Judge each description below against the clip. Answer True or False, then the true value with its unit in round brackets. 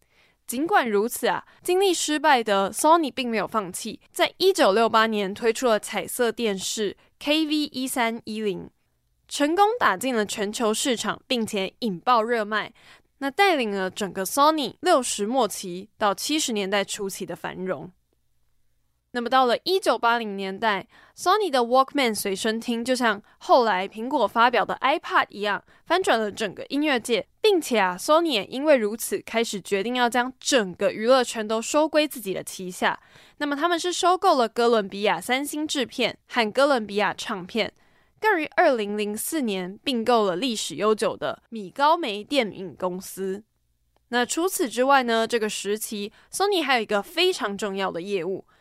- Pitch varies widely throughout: True (6.0 semitones)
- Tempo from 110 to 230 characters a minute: False (280 characters per minute)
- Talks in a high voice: True (230 Hz)